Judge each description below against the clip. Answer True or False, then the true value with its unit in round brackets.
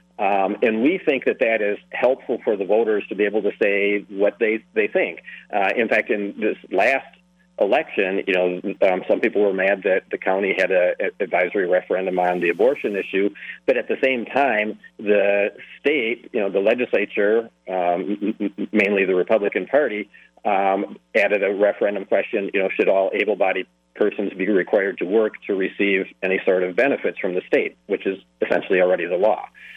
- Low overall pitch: True (105 Hz)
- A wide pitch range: True (5.7 semitones)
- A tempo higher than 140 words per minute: True (185 wpm)